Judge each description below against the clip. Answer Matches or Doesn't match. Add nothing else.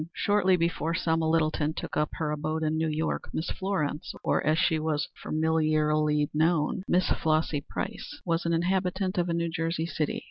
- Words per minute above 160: Matches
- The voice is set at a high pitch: Doesn't match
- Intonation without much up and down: Matches